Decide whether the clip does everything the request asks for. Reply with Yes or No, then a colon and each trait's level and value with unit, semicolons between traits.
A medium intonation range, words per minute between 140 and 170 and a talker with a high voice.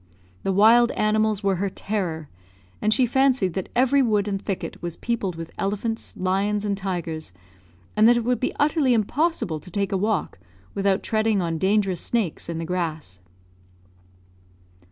Yes: average, 3.6 semitones; average, 160 wpm; high, 200 Hz